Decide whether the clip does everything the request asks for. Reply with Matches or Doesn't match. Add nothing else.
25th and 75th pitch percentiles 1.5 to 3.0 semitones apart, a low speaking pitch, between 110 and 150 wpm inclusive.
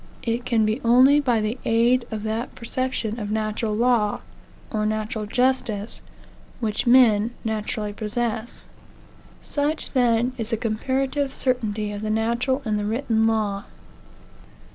Doesn't match